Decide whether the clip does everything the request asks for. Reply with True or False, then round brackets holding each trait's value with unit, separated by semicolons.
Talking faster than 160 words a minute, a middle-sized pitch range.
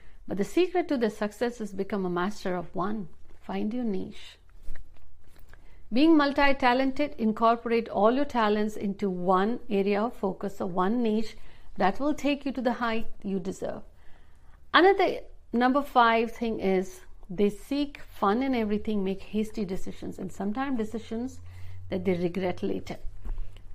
False (150 wpm; 4.2 semitones)